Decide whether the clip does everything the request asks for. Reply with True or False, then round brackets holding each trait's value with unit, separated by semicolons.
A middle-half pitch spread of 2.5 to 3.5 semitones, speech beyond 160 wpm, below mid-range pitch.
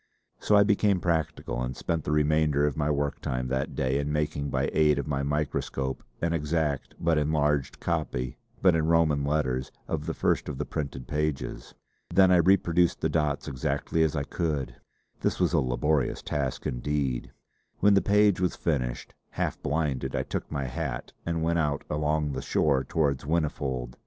True (2.9 semitones; 180 wpm; 75 Hz)